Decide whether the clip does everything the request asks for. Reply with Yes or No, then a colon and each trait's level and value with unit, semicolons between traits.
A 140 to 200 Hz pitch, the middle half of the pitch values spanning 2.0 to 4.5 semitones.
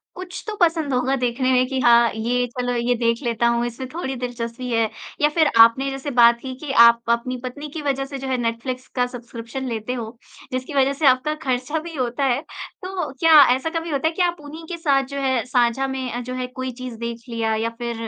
No: very high, 255 Hz; average, 2.8 semitones